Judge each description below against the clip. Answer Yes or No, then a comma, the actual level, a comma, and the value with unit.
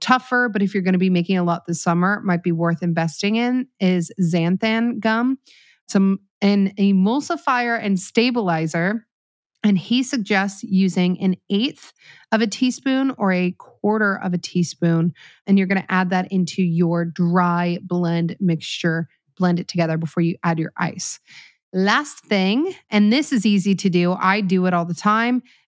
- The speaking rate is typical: Yes, average, 170 wpm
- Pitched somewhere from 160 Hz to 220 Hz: Yes, high, 190 Hz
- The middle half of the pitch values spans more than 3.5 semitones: Yes, average, 4.1 semitones